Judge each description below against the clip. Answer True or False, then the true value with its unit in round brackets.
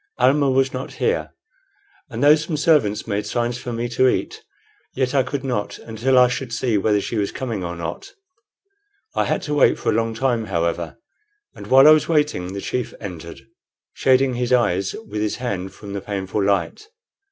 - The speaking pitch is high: False (120 Hz)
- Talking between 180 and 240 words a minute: True (190 wpm)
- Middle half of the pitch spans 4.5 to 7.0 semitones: True (4.8 semitones)